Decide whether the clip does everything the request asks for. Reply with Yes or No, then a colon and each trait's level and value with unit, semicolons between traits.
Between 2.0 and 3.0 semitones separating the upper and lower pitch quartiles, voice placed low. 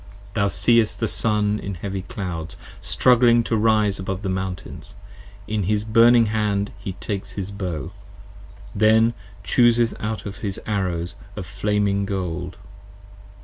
Yes: narrow, 2.6 semitones; low, 100 Hz